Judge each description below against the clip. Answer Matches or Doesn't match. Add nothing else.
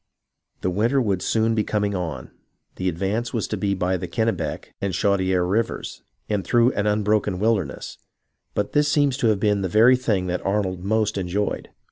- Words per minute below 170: Doesn't match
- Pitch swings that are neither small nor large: Matches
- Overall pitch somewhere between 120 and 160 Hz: Doesn't match